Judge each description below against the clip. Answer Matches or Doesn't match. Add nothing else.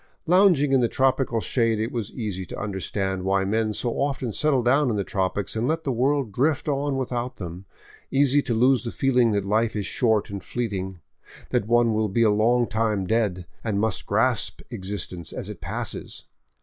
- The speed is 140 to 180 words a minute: Doesn't match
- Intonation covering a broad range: Doesn't match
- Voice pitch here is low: Matches